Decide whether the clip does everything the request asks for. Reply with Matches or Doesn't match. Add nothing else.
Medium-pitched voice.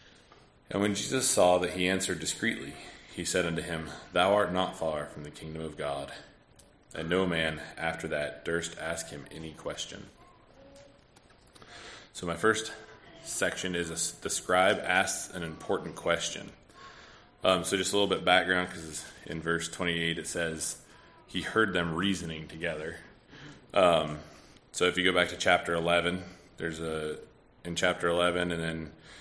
Doesn't match